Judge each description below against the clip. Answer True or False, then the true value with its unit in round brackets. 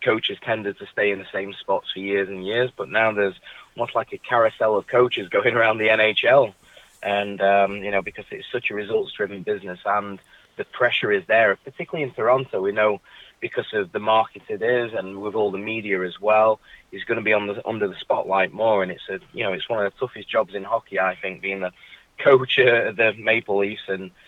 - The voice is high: False (105 Hz)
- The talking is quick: True (225 wpm)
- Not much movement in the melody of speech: True (2.0 semitones)